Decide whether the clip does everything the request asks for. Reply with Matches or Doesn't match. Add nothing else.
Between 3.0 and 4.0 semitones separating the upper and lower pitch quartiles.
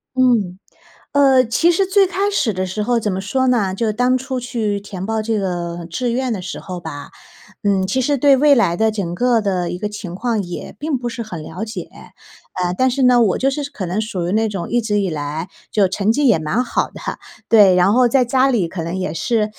Doesn't match